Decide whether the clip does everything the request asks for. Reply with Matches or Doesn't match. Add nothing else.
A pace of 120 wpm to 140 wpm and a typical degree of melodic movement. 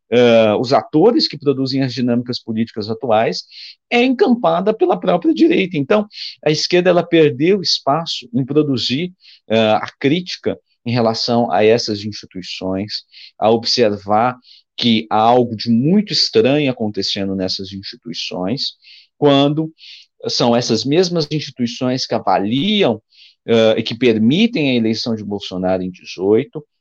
Doesn't match